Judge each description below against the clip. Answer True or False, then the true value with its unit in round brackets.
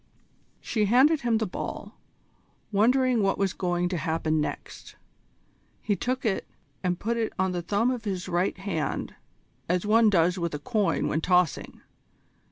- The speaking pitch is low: False (195 Hz)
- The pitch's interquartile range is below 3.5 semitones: False (4.2 semitones)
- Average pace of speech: True (160 wpm)